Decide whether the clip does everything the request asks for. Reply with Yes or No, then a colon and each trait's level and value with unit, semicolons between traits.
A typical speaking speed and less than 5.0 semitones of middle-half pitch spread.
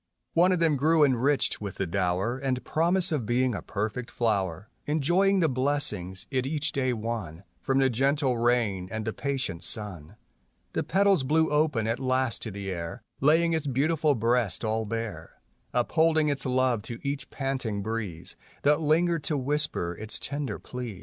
No: average, 170 wpm; wide, 5.4 semitones